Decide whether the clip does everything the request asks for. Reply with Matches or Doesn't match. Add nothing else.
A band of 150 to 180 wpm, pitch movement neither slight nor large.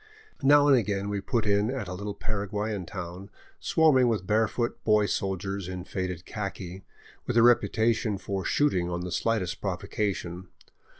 Matches